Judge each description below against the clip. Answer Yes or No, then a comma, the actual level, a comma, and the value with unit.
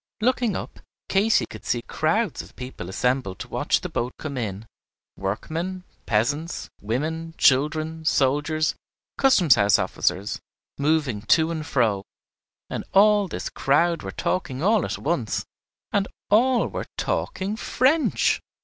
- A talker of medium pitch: Yes, medium, 155 Hz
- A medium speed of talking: No, slow, 130 wpm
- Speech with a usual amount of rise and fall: No, wide, 7.1 semitones